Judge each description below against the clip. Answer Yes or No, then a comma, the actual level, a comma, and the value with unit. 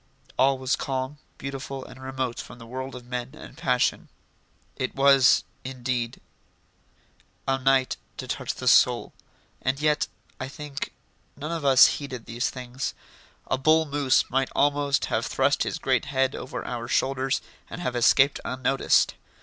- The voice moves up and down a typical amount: No, narrow, 1.4 semitones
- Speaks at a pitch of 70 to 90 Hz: No, low, 130 Hz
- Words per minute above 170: No, average, 150 wpm